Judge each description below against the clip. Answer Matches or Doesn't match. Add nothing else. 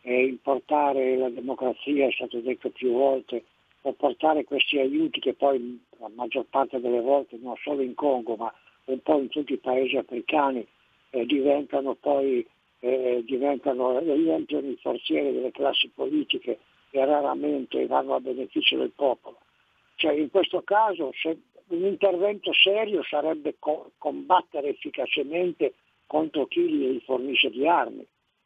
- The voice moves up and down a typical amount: Matches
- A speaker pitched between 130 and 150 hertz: Matches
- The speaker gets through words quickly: Doesn't match